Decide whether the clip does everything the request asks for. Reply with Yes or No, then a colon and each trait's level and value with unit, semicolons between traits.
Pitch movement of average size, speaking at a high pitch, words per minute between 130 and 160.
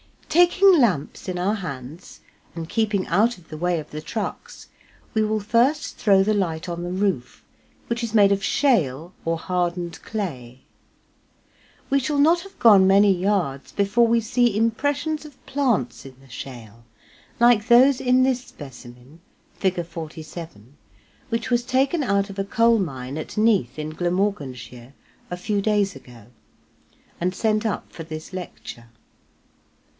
No: wide, 6.5 semitones; high, 195 Hz; average, 150 wpm